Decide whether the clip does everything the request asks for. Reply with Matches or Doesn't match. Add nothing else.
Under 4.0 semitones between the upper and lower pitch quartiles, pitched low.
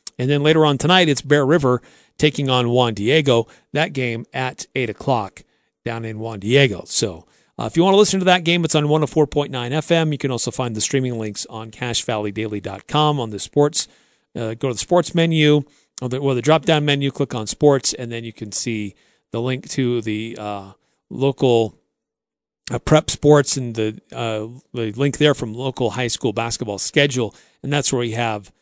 Doesn't match